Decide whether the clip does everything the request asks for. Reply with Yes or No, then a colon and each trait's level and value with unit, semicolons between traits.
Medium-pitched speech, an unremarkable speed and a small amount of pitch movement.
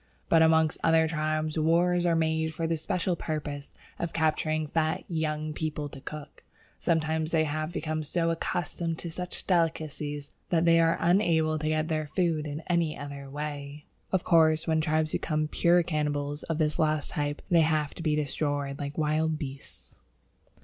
Yes: medium, 155 Hz; average, 170 wpm; narrow, 1.5 semitones